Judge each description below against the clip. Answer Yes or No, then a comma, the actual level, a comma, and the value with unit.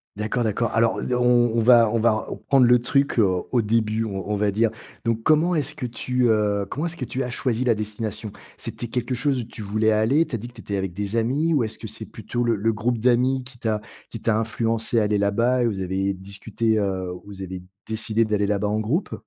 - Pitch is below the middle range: Yes, low, 115 Hz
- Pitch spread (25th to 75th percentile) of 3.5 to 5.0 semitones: No, average, 2.7 semitones